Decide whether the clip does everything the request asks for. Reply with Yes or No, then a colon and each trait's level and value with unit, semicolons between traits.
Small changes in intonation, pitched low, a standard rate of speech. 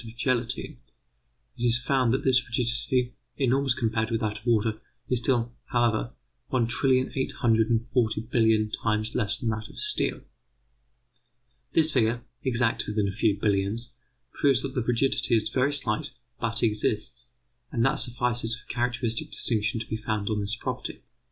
Yes: narrow, 2.3 semitones; low, 115 Hz; average, 165 wpm